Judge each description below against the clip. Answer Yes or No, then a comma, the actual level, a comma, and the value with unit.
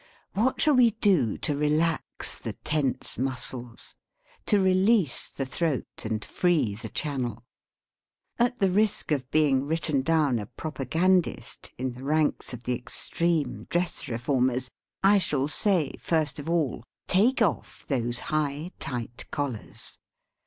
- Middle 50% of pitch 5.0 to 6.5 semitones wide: Yes, wide, 5.6 semitones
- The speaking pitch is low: No, medium, 150 Hz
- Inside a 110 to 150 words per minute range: Yes, slow, 135 wpm